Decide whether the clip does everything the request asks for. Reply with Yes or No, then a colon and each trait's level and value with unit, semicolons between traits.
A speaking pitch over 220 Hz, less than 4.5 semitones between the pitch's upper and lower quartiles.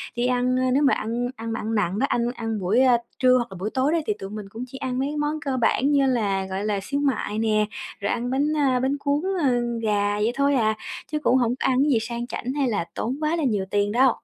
Yes: high, 245 Hz; average, 3.8 semitones